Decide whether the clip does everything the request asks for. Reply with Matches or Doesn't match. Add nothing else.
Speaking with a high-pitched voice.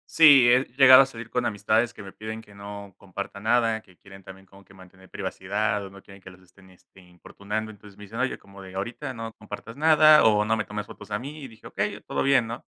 Doesn't match